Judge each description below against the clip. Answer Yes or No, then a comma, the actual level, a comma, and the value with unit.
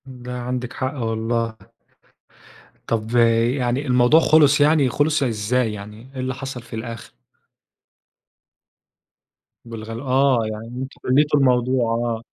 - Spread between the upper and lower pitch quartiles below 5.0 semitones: Yes, narrow, 2.5 semitones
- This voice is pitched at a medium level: No, low, 125 Hz